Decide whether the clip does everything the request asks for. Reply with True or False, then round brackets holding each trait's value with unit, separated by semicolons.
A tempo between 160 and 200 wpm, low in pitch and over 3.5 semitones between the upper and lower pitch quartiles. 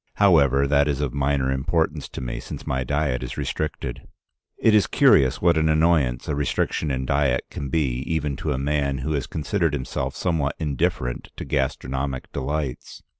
False (175 wpm; 70 Hz; 2.9 semitones)